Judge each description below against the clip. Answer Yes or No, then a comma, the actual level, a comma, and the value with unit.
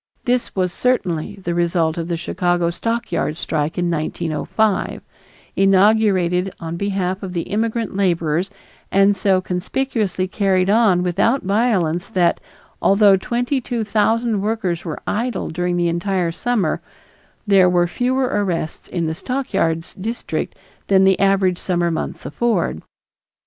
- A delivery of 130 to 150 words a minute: Yes, slow, 135 wpm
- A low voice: No, high, 190 Hz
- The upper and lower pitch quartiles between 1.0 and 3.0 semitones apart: No, average, 3.7 semitones